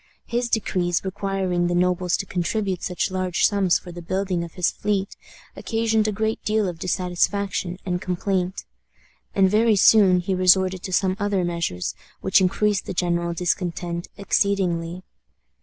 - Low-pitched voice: No, medium, 185 Hz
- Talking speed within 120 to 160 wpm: Yes, average, 150 wpm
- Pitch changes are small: Yes, narrow, 2.1 semitones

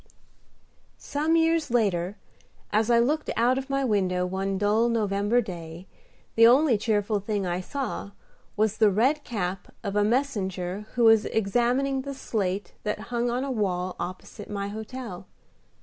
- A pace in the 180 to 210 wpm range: No, average, 155 wpm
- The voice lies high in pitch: Yes, high, 215 Hz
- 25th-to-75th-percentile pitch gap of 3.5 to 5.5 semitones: Yes, average, 4.0 semitones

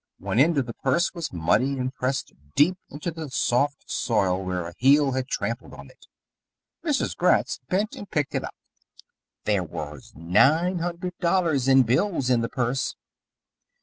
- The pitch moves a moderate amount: No, wide, 6.3 semitones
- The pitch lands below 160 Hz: Yes, low, 135 Hz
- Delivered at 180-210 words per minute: No, average, 165 wpm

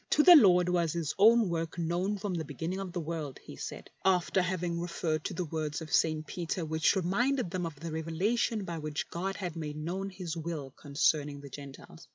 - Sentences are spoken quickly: Yes, fast, 215 wpm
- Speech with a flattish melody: No, average, 3.0 semitones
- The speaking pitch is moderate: Yes, medium, 170 Hz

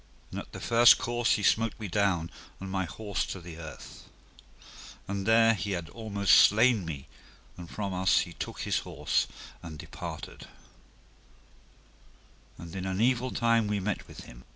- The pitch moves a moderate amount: Yes, average, 4.4 semitones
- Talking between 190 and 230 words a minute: No, average, 165 wpm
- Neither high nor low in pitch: No, low, 100 Hz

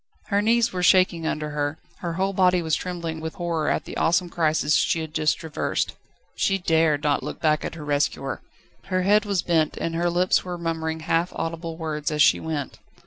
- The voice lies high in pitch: No, medium, 165 Hz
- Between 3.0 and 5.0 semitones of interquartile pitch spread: No, narrow, 2.6 semitones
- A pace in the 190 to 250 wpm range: Yes, average, 200 wpm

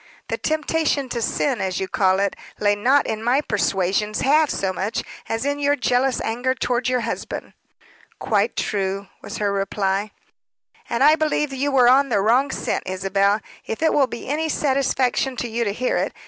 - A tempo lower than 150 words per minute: No, average, 185 wpm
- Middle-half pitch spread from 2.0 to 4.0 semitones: No, average, 5.3 semitones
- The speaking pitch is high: Yes, high, 240 Hz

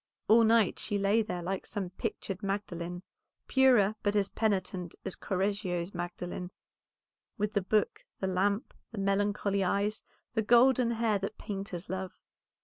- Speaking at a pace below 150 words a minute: Yes, average, 140 wpm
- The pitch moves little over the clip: Yes, narrow, 2.3 semitones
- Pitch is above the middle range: Yes, high, 200 Hz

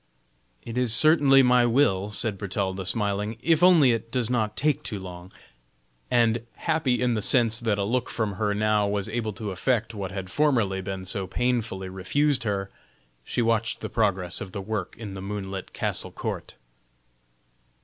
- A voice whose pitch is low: Yes, low, 110 Hz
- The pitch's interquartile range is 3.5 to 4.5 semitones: Yes, average, 3.9 semitones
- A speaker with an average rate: Yes, average, 170 wpm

